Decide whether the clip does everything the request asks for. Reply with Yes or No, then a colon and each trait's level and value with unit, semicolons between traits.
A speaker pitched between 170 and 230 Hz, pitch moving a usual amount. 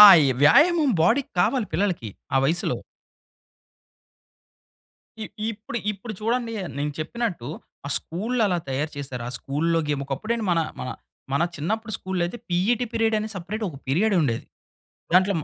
No: high, 190 Hz; wide, 7.0 semitones